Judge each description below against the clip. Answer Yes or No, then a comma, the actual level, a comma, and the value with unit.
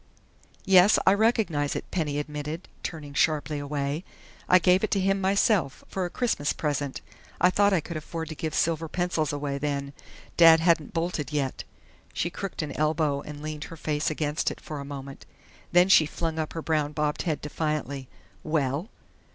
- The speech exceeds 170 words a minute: Yes, average, 180 wpm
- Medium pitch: Yes, medium, 155 Hz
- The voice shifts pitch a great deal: No, average, 3.1 semitones